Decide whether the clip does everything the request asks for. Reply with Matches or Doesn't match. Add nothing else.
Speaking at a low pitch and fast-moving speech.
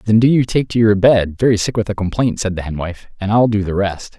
Matches